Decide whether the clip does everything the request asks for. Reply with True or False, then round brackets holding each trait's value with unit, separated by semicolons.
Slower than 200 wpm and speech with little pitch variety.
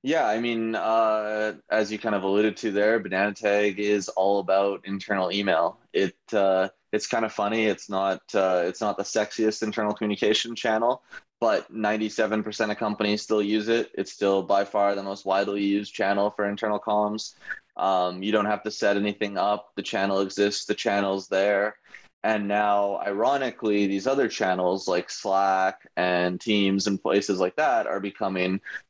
True (175 wpm; 1.6 semitones)